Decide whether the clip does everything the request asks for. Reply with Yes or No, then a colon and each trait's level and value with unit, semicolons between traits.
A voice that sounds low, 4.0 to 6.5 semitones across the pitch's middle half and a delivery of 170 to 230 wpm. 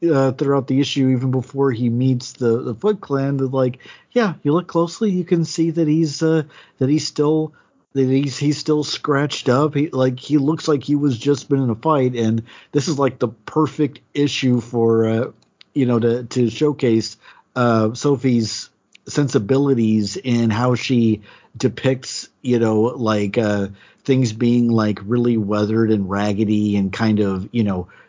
Yes: low, 130 Hz; average, 4.3 semitones; average, 175 wpm